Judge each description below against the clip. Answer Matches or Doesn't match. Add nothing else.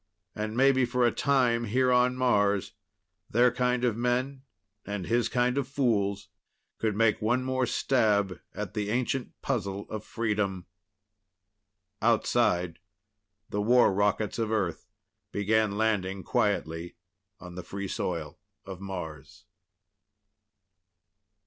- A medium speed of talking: Doesn't match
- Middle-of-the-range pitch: Doesn't match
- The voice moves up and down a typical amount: Matches